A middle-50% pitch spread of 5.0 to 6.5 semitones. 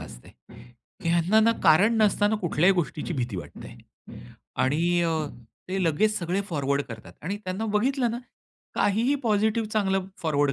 Yes: wide, 5.4 semitones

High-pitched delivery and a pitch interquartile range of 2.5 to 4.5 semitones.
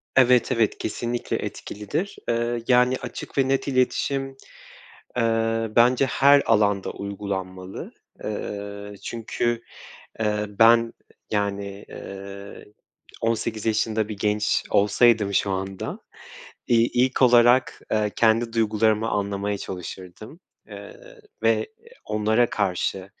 No: low, 110 Hz; average, 2.9 semitones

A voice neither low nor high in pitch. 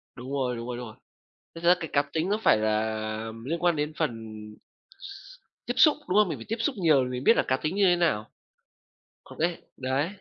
Yes: medium, 155 Hz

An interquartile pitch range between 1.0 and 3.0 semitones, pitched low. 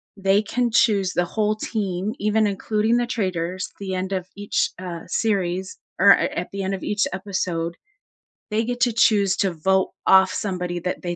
No: narrow, 2.6 semitones; high, 195 Hz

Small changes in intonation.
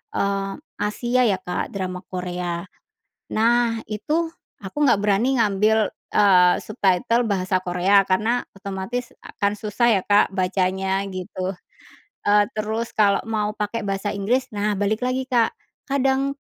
No: average, 3.2 semitones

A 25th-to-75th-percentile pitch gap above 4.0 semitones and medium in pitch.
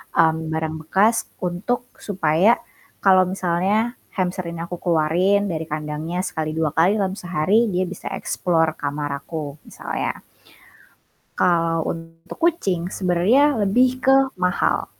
No: average, 3.6 semitones; medium, 180 Hz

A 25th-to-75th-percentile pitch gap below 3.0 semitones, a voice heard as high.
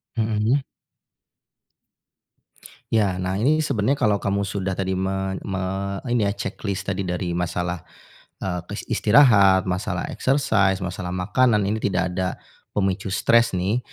No: narrow, 2.4 semitones; low, 100 Hz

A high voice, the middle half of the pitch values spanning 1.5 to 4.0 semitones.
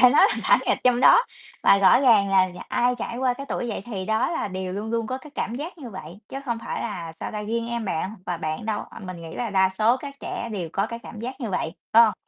No: high, 220 Hz; average, 4.4 semitones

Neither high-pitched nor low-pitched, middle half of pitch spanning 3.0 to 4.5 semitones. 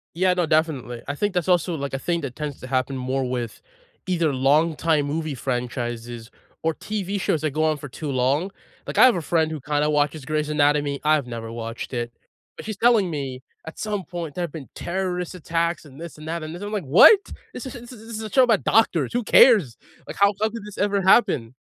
No: medium, 155 Hz; wide, 5.4 semitones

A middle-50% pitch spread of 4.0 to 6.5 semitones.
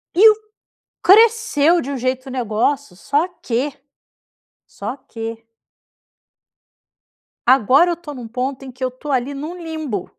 Yes: average, 4.3 semitones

